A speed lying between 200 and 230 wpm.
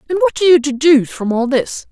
No: fast, 250 wpm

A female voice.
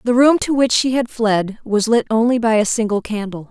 Yes: female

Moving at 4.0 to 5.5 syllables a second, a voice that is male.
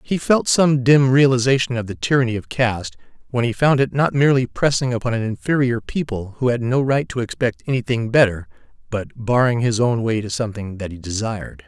No: 5.7 syllables/s; male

